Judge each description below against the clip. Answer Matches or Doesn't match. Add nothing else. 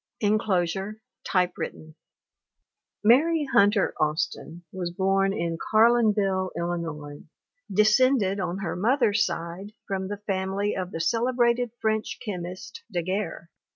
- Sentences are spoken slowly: Matches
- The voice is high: Matches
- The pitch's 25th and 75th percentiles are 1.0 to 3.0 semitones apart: Doesn't match